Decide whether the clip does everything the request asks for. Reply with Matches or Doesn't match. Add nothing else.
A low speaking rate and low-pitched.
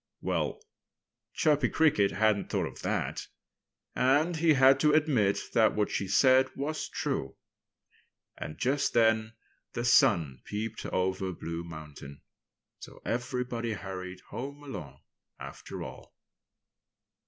Matches